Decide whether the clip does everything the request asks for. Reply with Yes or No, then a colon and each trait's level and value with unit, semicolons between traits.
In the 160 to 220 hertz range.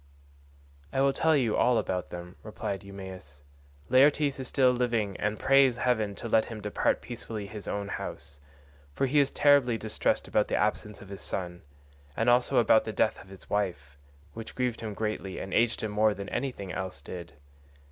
No: low, 110 Hz